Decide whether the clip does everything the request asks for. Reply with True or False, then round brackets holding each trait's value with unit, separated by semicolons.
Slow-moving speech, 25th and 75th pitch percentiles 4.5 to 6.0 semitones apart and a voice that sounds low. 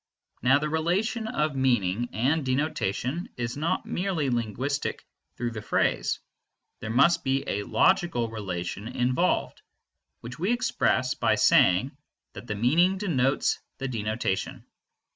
True (125 wpm; 5.6 semitones; 130 Hz)